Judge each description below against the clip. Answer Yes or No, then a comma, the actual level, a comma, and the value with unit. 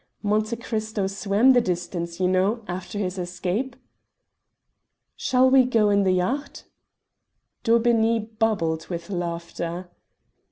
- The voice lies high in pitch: Yes, high, 200 Hz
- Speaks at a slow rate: Yes, slow, 115 wpm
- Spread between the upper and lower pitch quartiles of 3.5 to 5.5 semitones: Yes, average, 4.2 semitones